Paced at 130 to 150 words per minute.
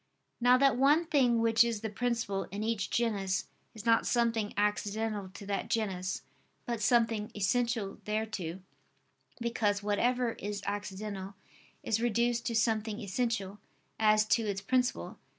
Yes: slow, 135 wpm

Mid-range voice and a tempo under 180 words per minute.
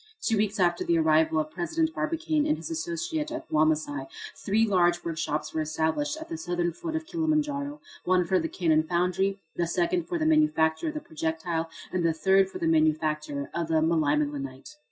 No: medium, 175 Hz; average, 185 wpm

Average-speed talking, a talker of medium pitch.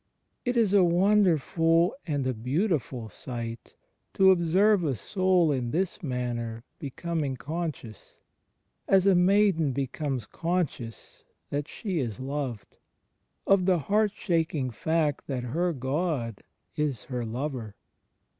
No: slow, 125 wpm; medium, 150 Hz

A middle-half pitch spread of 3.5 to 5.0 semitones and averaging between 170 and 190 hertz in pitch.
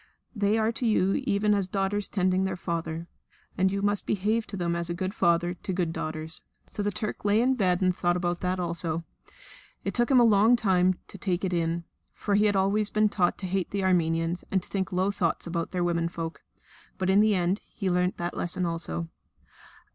No: average, 2.8 semitones; medium, 185 Hz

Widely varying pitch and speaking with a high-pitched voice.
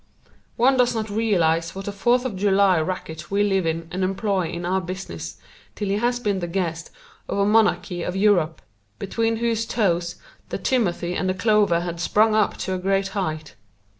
No: average, 3.5 semitones; high, 195 Hz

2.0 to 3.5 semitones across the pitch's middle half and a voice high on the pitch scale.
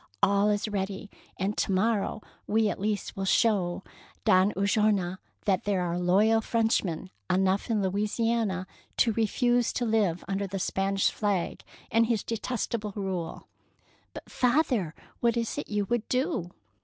Yes: average, 2.9 semitones; high, 205 Hz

